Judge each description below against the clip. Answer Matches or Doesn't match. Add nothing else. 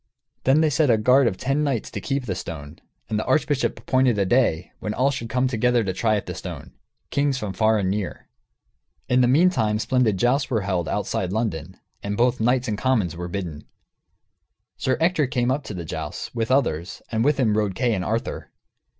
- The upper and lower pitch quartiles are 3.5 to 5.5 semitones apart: Matches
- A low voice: Matches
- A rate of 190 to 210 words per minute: Matches